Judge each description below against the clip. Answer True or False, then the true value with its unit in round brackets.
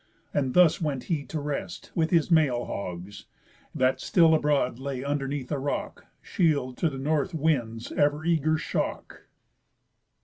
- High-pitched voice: False (145 Hz)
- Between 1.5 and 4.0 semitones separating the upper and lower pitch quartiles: True (3.4 semitones)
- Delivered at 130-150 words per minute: True (145 wpm)